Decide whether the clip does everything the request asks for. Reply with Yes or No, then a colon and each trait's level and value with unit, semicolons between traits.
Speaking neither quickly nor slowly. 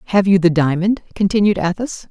Yes: average, 170 wpm